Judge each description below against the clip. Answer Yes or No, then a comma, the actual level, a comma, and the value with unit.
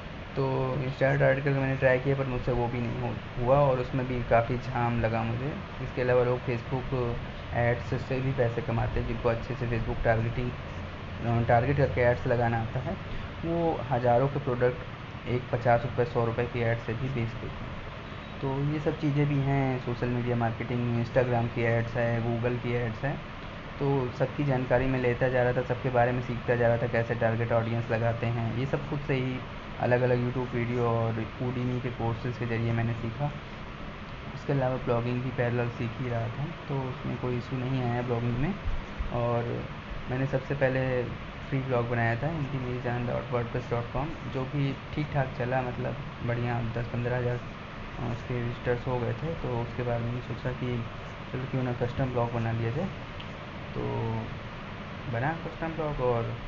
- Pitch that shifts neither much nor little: No, narrow, 1.8 semitones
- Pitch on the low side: Yes, low, 120 Hz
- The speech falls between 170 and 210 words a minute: Yes, average, 185 wpm